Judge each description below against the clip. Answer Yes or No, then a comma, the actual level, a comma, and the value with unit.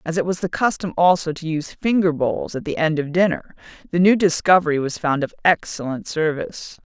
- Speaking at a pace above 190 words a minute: Yes, average, 200 wpm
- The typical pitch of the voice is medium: Yes, medium, 165 Hz